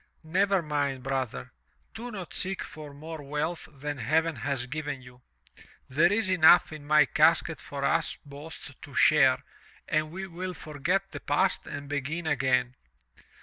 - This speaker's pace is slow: No, average, 150 wpm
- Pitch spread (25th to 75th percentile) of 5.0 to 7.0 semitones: No, average, 3.7 semitones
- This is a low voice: No, medium, 150 Hz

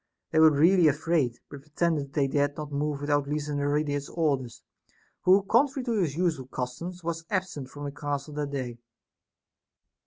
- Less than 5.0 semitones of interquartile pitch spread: Yes, average, 2.8 semitones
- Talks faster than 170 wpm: No, average, 160 wpm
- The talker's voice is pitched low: No, medium, 145 Hz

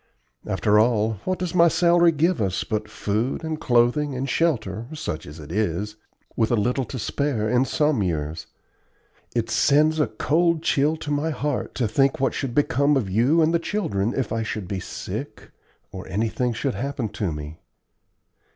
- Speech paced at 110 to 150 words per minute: No, average, 180 wpm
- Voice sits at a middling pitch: No, low, 125 Hz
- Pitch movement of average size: No, wide, 5.9 semitones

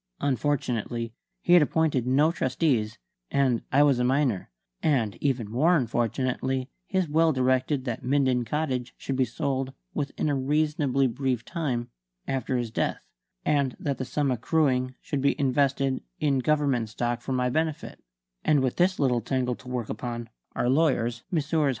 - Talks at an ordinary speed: Yes, average, 155 wpm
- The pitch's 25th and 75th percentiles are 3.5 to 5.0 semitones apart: No, average, 2.9 semitones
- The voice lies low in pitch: Yes, low, 130 Hz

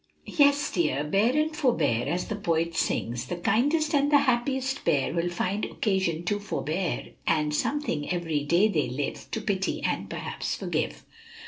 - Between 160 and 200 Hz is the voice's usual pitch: Yes, high, 190 Hz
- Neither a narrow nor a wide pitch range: No, wide, 8.5 semitones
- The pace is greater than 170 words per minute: No, average, 160 wpm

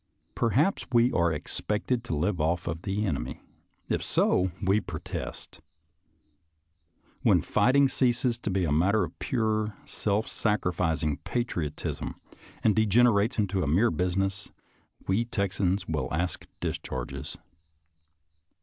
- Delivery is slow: Yes, slow, 120 wpm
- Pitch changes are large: No, average, 4.4 semitones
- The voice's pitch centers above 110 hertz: No, very low, 95 Hz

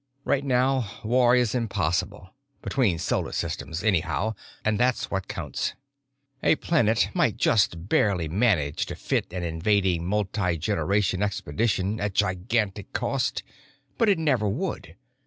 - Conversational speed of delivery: No, slow, 120 wpm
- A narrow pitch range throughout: No, average, 4.9 semitones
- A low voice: Yes, low, 105 Hz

